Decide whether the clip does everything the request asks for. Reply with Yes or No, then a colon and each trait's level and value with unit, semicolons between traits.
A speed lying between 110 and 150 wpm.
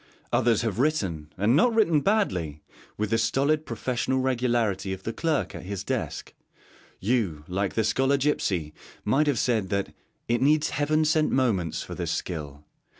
No: average, 160 wpm